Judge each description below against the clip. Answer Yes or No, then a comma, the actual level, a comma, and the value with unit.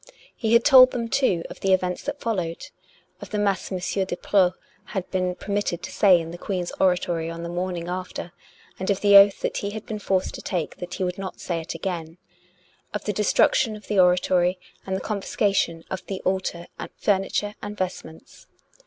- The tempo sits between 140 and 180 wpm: No, average, 200 wpm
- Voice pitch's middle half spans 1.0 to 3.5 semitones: Yes, narrow, 2.4 semitones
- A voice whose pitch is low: No, high, 190 Hz